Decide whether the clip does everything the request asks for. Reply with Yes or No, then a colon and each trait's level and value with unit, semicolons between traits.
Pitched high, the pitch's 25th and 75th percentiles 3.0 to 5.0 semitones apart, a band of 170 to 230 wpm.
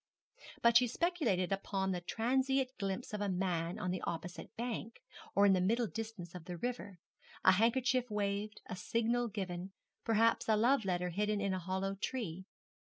Yes: high, 205 Hz; average, 3.9 semitones; average, 175 wpm